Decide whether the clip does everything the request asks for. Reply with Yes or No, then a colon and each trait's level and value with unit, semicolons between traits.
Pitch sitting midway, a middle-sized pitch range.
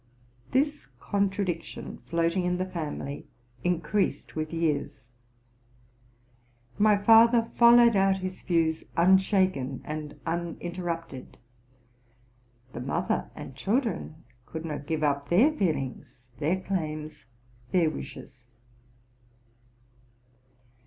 Yes: medium, 170 Hz; average, 4.1 semitones